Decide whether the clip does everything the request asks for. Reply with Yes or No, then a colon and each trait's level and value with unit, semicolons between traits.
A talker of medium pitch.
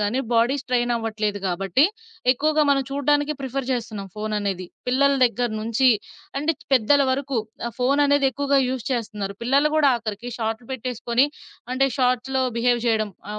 No: very high, 250 Hz